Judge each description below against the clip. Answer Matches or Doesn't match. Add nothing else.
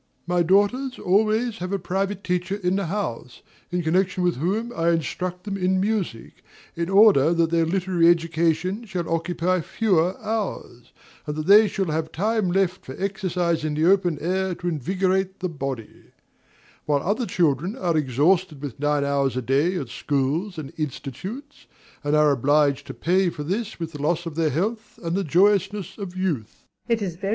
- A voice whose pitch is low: Doesn't match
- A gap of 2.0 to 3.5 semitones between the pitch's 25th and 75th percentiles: Doesn't match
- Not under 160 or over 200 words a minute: Matches